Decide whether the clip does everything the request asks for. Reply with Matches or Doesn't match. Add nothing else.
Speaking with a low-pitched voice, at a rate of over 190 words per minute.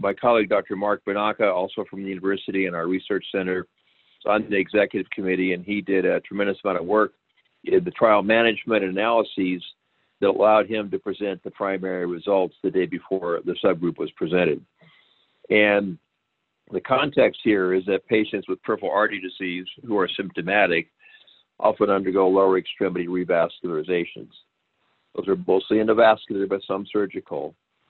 Doesn't match